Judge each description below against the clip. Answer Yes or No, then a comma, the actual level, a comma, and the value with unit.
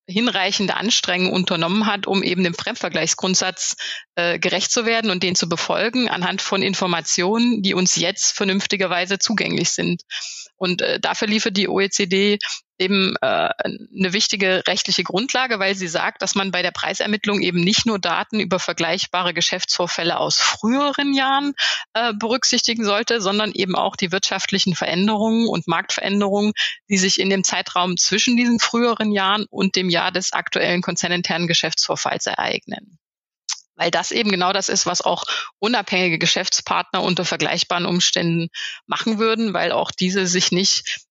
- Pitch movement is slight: No, average, 3.1 semitones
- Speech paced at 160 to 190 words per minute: No, average, 150 wpm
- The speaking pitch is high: Yes, high, 195 Hz